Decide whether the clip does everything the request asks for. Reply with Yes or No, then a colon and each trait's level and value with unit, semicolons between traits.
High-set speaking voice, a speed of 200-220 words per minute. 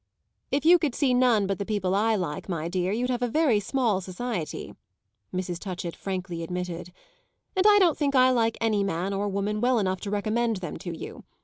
Yes: high, 205 Hz; fast, 205 wpm